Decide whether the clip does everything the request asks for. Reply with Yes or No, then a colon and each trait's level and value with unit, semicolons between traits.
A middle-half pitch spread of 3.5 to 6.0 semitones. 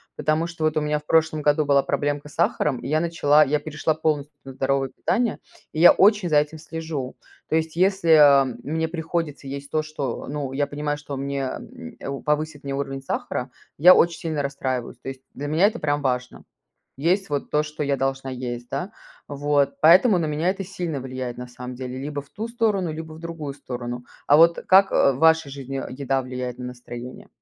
No: average, 3.0 semitones